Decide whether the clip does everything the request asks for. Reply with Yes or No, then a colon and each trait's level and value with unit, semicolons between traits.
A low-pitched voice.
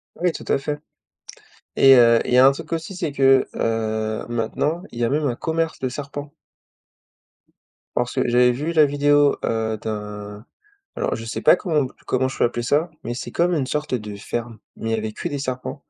Yes: low, 130 Hz